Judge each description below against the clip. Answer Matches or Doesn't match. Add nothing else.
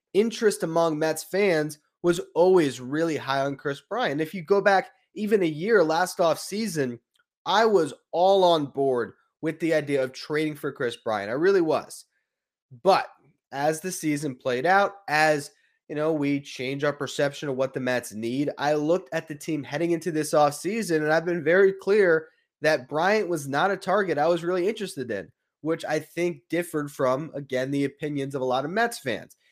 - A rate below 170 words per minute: Doesn't match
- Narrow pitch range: Doesn't match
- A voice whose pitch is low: Doesn't match